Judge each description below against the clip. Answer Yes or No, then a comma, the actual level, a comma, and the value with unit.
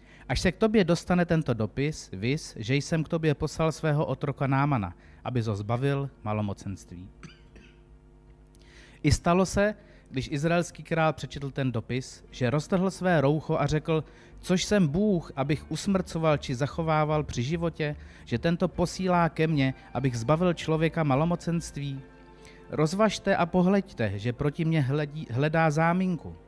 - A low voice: No, medium, 155 Hz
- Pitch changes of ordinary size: Yes, average, 4.6 semitones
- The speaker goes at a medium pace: Yes, average, 145 wpm